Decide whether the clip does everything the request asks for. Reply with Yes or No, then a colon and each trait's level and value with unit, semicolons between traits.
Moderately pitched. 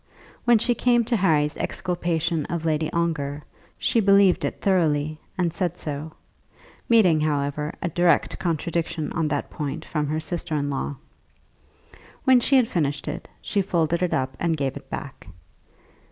Yes: medium, 165 Hz